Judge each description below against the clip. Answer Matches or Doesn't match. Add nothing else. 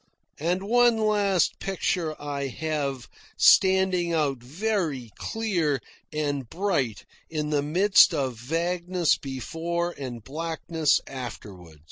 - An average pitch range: Matches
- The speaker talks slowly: Matches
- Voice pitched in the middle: Matches